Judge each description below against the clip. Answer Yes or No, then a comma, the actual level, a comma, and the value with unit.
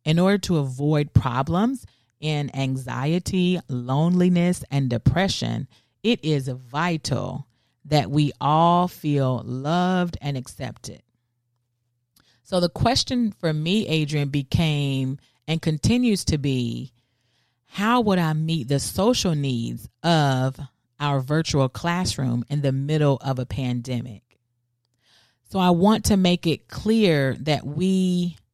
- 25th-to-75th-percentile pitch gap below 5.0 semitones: No, wide, 5.5 semitones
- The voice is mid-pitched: Yes, medium, 145 Hz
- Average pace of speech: No, slow, 120 wpm